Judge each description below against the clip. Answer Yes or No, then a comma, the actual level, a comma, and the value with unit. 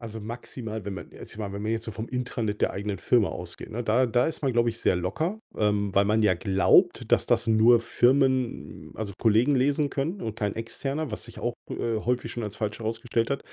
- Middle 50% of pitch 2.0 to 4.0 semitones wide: Yes, average, 2.9 semitones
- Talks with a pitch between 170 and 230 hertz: No, low, 115 Hz